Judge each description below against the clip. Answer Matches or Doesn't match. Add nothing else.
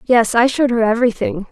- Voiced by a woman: Matches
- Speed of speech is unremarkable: Matches